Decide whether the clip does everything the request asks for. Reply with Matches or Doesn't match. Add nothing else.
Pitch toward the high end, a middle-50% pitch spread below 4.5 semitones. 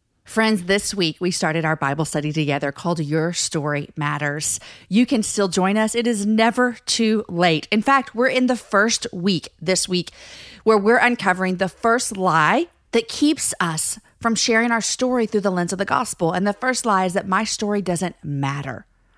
Doesn't match